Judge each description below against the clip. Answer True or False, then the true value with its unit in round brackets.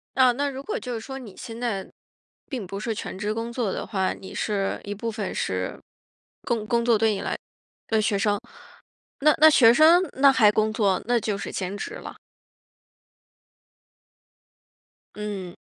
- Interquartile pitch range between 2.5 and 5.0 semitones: True (3.3 semitones)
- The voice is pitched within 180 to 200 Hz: False (220 Hz)